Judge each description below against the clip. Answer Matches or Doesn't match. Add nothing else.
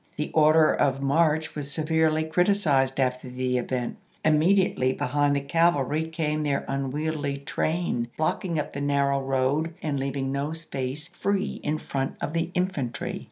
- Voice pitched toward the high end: Doesn't match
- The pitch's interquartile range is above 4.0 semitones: Doesn't match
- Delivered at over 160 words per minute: Doesn't match